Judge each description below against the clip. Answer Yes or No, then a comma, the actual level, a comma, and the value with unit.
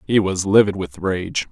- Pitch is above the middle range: No, low, 100 Hz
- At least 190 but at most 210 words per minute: Yes, average, 200 wpm